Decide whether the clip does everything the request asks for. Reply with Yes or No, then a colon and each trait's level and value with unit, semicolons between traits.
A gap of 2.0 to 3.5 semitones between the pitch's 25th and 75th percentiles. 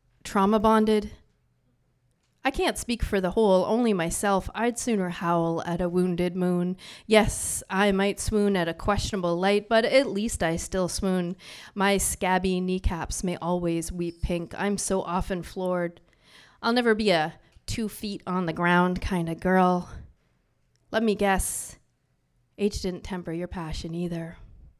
Yes: average, 2.8 semitones